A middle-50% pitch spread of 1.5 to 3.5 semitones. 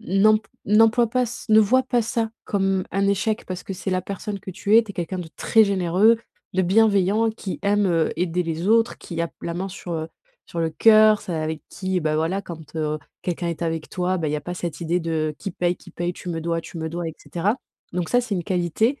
No: average, 4.0 semitones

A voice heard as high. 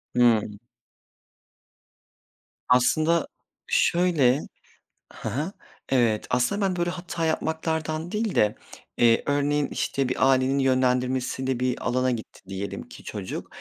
No: low, 130 Hz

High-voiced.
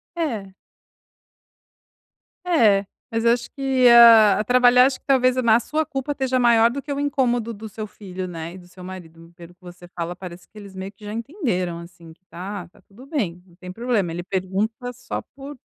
Yes: high, 215 Hz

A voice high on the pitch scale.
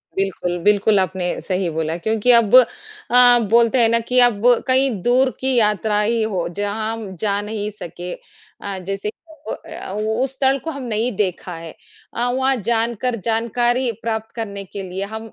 Yes: high, 220 Hz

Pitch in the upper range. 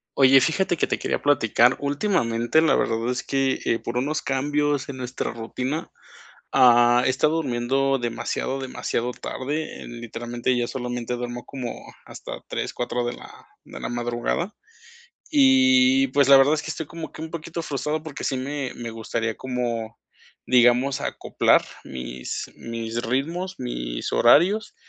No: low, 130 Hz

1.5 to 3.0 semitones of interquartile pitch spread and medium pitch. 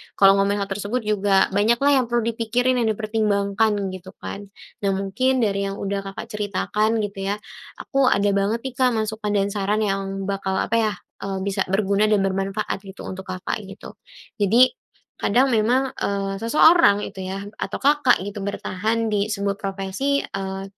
No: narrow, 2.4 semitones; high, 205 Hz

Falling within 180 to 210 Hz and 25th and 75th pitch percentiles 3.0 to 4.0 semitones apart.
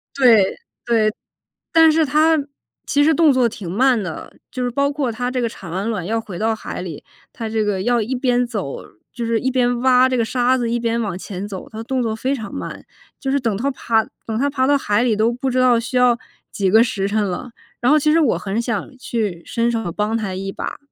No: high, 235 Hz; average, 3.3 semitones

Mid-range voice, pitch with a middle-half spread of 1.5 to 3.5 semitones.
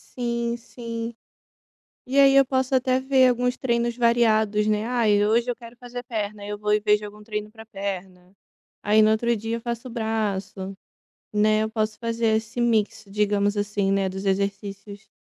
No: high, 220 Hz; narrow, 2.4 semitones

